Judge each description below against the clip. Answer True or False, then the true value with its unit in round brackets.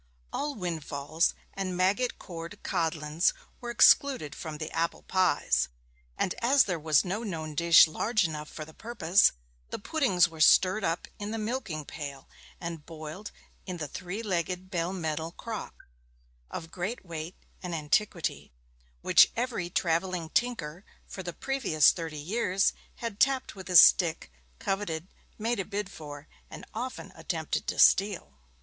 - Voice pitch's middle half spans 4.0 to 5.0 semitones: True (4.4 semitones)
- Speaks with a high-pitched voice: False (180 Hz)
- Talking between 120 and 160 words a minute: True (150 wpm)